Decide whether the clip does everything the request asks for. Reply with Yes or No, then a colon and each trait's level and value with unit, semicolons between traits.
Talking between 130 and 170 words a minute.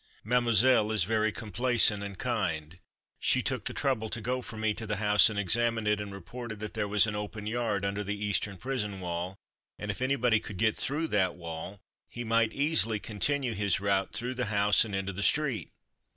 No: average, 200 wpm